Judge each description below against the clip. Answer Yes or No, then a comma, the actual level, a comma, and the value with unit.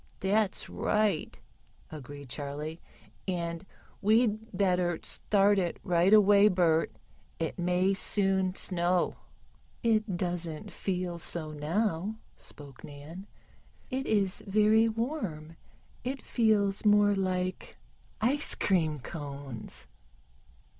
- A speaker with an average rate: No, slow, 100 wpm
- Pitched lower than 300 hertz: Yes, medium, 185 Hz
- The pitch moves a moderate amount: Yes, average, 4.0 semitones